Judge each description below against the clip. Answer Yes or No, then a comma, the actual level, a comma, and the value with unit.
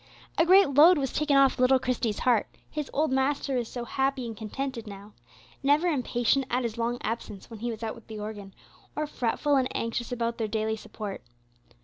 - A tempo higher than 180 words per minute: Yes, average, 200 wpm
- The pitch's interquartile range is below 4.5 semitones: Yes, average, 3.6 semitones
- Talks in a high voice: Yes, high, 245 Hz